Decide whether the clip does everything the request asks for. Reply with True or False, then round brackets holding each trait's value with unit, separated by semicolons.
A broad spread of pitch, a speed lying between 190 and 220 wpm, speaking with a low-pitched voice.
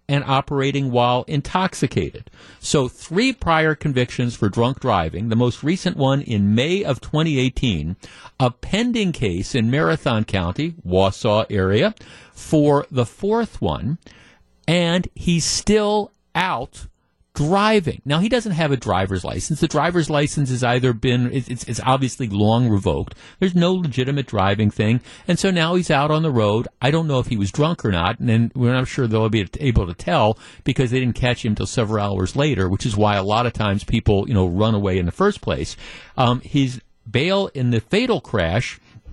False (6.1 semitones; 180 wpm; 125 Hz)